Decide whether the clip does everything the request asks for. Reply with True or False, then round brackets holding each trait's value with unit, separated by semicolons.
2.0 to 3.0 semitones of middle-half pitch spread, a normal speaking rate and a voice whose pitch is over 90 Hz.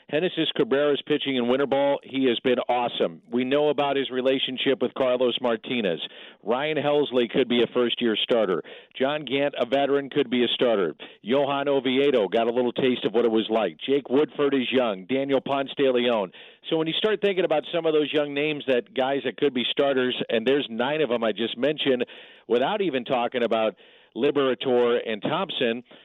True (2.7 semitones; 195 wpm; 135 Hz)